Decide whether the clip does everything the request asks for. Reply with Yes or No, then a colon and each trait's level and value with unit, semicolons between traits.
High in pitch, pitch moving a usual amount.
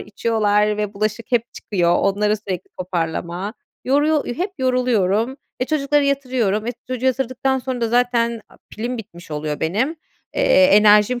Yes: high, 225 Hz; average, 4.0 semitones